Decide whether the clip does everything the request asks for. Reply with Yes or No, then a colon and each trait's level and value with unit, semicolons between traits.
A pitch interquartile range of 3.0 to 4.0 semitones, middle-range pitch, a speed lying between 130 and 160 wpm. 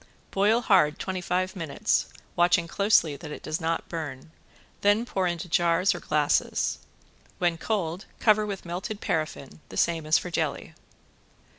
Yes: average, 3.3 semitones; medium, 175 Hz; average, 150 wpm